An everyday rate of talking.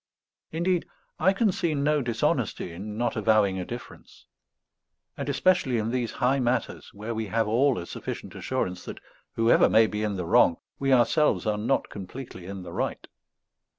Yes: average, 170 wpm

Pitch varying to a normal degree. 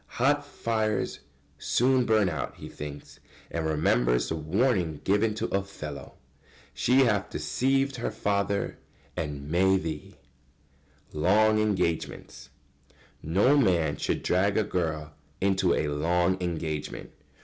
No: wide, 5.7 semitones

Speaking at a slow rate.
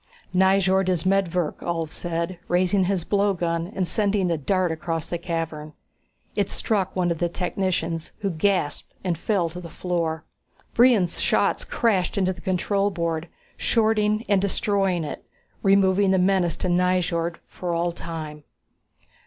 No: average, 145 wpm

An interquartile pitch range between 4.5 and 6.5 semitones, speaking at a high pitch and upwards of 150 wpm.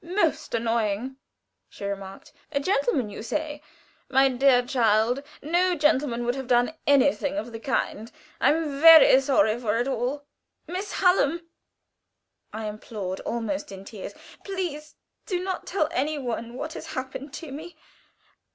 No: average, 4.9 semitones; very high, 270 Hz; average, 145 wpm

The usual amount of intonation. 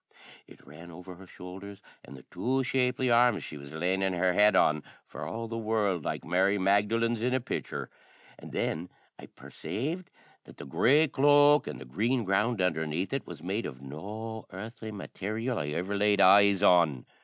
Yes: average, 4.7 semitones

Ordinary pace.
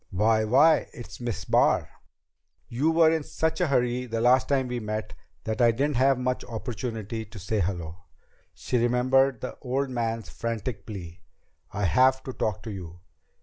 Yes: average, 170 wpm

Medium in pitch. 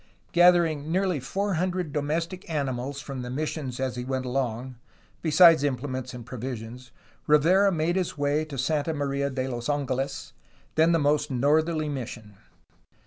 Yes: medium, 145 Hz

